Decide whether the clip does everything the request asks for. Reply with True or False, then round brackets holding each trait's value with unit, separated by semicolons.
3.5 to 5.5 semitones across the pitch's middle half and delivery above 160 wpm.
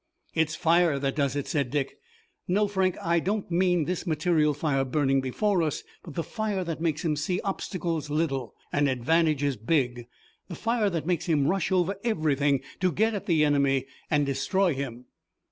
True (4.2 semitones; 180 wpm)